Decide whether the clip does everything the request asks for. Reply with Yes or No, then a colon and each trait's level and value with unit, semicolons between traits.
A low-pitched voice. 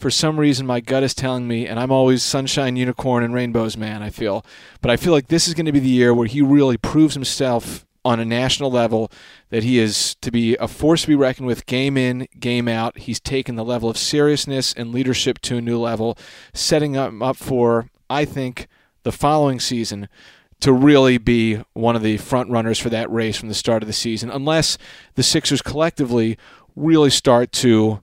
Yes: low, 125 Hz